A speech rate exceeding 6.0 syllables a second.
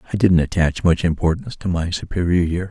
Yes: 6.2 syllables/s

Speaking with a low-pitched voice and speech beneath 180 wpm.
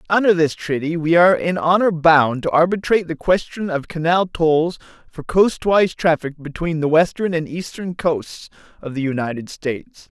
No: medium, 165 Hz; average, 165 wpm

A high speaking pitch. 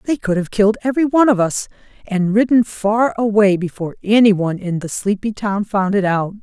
Yes: high, 205 Hz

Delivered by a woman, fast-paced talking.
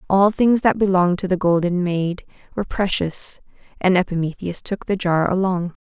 No: female; average, 165 wpm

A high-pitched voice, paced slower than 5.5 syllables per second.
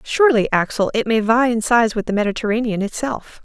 No: high, 225 Hz; 5.9 syllables/s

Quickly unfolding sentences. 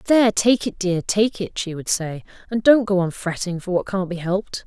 Yes: fast, 245 wpm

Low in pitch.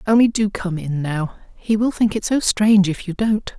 No: high, 200 Hz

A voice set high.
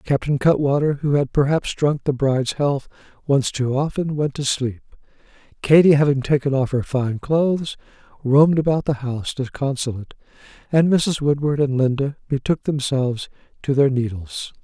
No: medium, 140 Hz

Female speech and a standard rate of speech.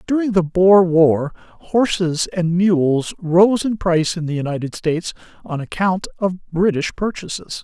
No: male; average, 150 wpm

